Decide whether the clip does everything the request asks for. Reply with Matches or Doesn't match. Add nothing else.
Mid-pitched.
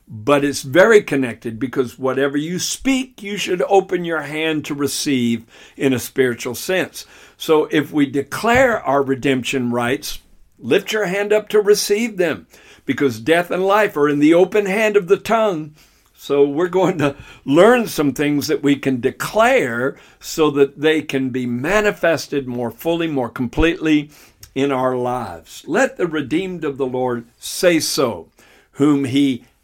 Matches